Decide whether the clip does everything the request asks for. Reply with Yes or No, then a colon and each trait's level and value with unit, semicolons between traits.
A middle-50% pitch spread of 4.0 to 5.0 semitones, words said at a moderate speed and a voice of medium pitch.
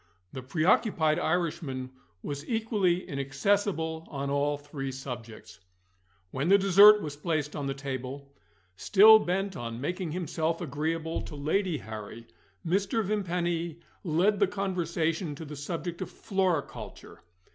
No: average, 4.7 semitones; slow, 125 wpm; medium, 160 Hz